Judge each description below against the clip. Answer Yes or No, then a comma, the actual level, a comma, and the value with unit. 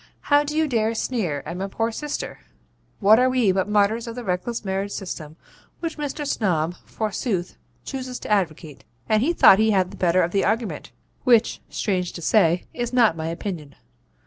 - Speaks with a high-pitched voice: Yes, high, 210 Hz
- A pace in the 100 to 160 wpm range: No, average, 185 wpm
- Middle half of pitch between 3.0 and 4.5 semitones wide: No, average, 5.1 semitones